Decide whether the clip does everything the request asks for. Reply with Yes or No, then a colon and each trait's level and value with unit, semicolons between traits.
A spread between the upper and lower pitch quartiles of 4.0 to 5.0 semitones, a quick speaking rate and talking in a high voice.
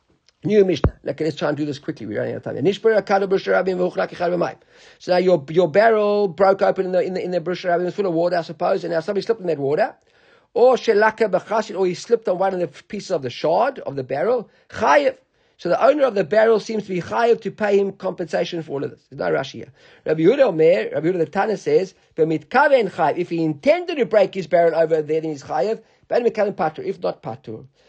Yes: average, 4.3 semitones; fast, 220 wpm; high, 195 Hz